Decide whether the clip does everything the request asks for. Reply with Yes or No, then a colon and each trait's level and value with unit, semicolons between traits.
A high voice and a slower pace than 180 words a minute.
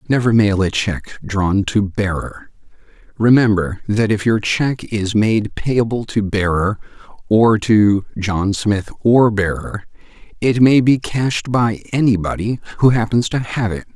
No: low, 110 Hz; average, 145 wpm